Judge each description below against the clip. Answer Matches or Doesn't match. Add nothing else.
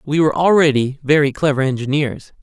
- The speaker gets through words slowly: Doesn't match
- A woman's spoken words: Doesn't match